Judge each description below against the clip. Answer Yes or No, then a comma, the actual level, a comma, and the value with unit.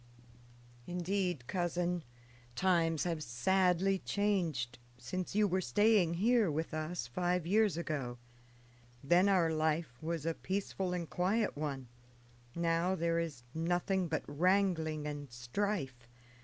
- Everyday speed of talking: No, slow, 120 wpm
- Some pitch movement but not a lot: Yes, average, 3.4 semitones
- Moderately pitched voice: Yes, medium, 170 Hz